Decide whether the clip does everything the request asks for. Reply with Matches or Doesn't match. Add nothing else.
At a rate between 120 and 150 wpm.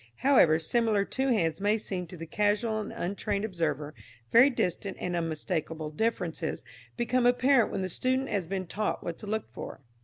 Doesn't match